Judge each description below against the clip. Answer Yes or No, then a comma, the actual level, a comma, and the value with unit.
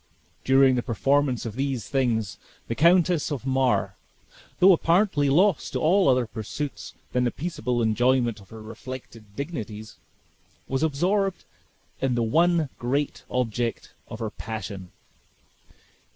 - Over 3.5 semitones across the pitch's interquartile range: Yes, average, 4.6 semitones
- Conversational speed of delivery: No, slow, 130 wpm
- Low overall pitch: Yes, low, 130 Hz